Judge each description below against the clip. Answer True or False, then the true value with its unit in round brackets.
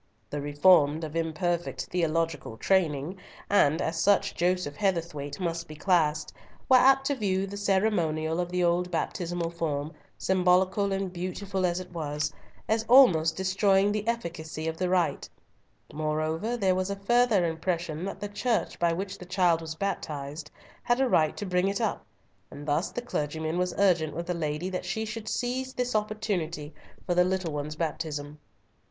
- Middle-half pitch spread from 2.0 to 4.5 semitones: True (3.8 semitones)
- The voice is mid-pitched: True (180 Hz)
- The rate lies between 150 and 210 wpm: True (170 wpm)